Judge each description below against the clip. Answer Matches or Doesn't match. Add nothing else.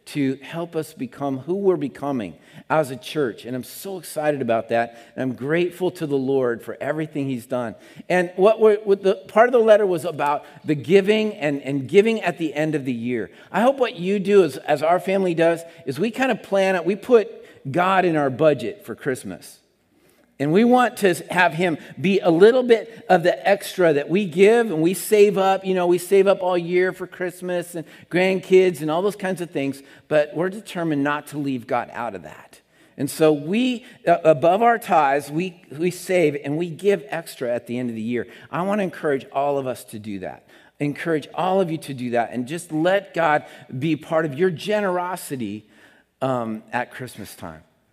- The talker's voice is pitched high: Doesn't match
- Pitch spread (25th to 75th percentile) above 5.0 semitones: Matches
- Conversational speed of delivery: Doesn't match